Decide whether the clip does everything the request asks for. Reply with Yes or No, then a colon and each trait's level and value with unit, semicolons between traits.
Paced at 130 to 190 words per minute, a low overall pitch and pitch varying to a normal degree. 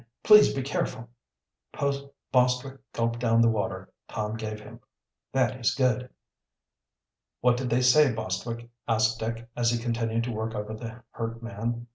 No: average, 150 wpm; low, 115 Hz; narrow, 1.8 semitones